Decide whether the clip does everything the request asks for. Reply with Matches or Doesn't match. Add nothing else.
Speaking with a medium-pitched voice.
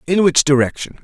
Matches